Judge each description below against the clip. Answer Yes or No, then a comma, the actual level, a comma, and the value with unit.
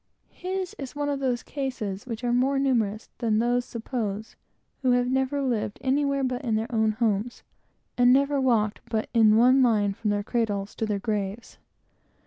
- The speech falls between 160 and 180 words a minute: Yes, average, 175 wpm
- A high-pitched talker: Yes, high, 240 Hz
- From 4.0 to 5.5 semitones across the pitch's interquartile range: No, average, 3.5 semitones